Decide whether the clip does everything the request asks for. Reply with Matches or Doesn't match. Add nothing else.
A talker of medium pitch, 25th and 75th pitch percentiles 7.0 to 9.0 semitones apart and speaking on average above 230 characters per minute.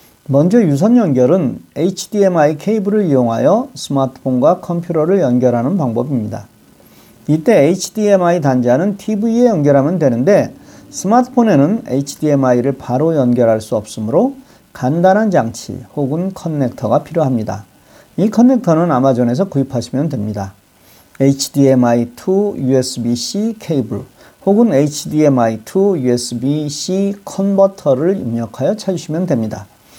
Matches